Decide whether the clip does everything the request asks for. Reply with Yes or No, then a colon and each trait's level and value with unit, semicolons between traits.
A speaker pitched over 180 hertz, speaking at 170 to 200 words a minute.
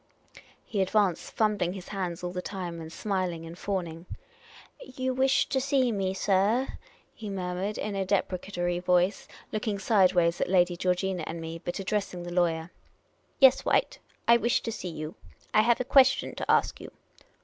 Yes: high, 190 Hz; average, 180 wpm